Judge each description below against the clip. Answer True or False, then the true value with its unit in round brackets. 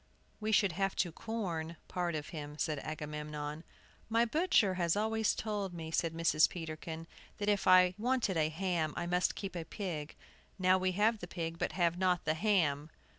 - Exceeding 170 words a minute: True (180 wpm)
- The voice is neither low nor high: True (175 Hz)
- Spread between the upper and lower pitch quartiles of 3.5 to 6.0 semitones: True (3.9 semitones)